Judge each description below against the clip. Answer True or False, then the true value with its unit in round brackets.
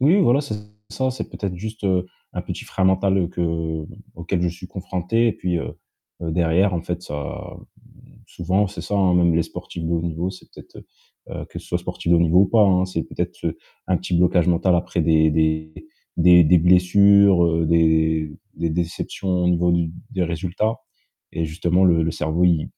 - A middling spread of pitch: False (2.2 semitones)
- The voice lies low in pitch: True (90 Hz)